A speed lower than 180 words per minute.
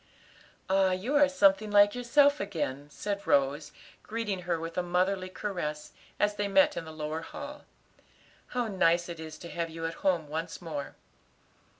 Yes: average, 170 wpm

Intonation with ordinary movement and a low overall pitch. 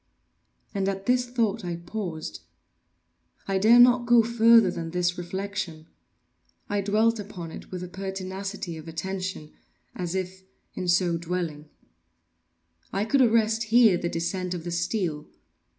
No: average, 3.9 semitones; high, 190 Hz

